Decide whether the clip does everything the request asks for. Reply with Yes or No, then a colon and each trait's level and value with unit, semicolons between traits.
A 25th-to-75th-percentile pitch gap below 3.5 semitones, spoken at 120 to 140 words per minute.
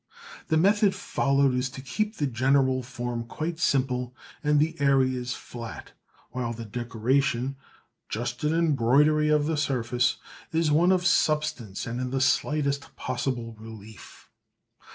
No: average, 3.8 semitones; slow, 135 wpm